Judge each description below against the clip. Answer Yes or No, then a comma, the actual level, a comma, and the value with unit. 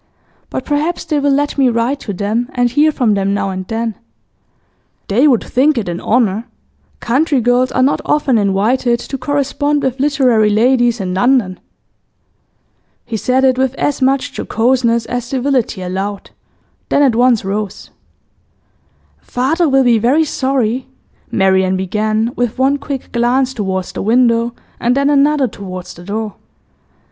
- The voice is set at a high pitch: Yes, high, 245 Hz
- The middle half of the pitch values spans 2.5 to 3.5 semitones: No, average, 4.0 semitones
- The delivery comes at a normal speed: Yes, average, 155 wpm